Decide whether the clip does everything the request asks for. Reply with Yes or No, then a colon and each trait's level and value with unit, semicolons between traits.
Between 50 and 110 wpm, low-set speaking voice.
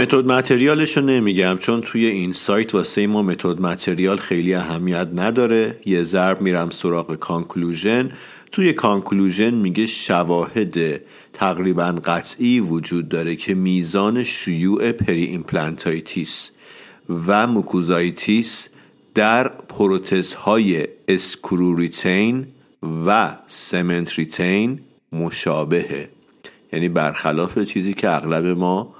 Yes: slow, 105 wpm; very low, 95 Hz